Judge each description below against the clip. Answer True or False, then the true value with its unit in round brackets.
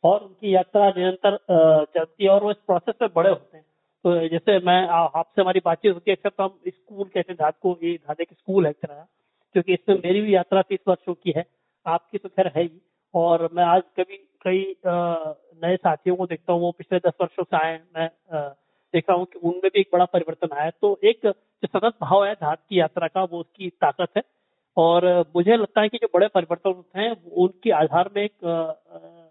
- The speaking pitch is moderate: True (180 Hz)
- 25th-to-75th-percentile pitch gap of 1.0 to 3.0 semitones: True (2.6 semitones)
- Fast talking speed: True (205 wpm)